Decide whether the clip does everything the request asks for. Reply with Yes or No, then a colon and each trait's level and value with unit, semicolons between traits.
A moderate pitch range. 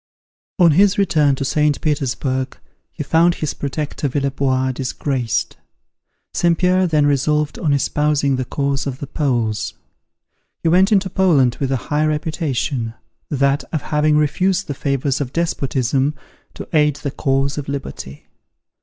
No: narrow, 2.3 semitones